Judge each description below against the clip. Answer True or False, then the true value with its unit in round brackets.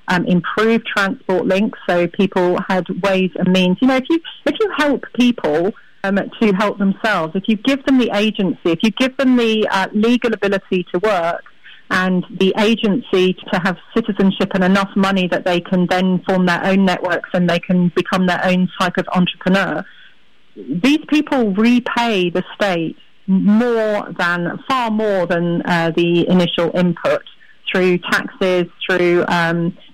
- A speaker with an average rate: True (165 wpm)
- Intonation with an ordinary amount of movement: True (3.5 semitones)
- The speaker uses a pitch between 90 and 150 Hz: False (190 Hz)